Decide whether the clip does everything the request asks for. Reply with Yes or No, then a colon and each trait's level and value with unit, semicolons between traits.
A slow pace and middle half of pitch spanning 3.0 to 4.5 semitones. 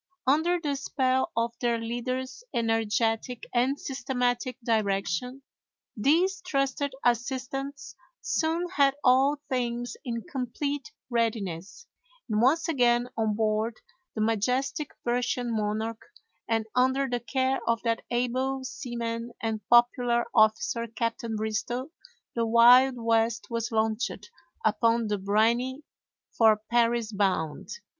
No: slow, 115 wpm; narrow, 2.6 semitones